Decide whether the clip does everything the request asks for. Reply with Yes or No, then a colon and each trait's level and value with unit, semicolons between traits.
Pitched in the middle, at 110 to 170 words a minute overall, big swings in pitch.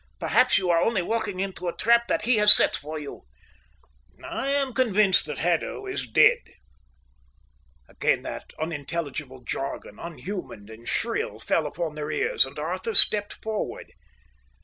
Yes: medium, 175 Hz; average, 150 wpm; wide, 6.0 semitones